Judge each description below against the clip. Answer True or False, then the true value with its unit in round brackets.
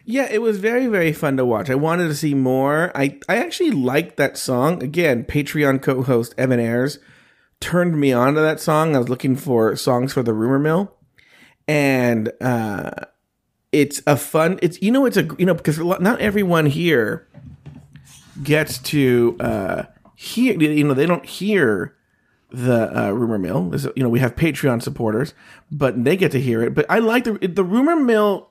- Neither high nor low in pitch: True (145 Hz)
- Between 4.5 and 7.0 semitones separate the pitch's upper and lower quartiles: True (5.6 semitones)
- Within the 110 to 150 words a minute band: False (190 wpm)